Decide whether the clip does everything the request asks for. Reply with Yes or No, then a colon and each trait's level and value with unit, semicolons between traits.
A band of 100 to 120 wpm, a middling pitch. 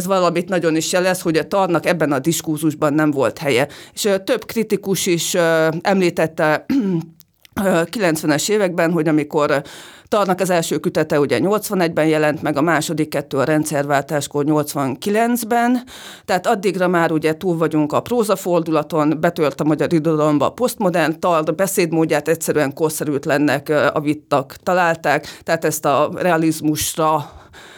No: average, 135 wpm; medium, 165 Hz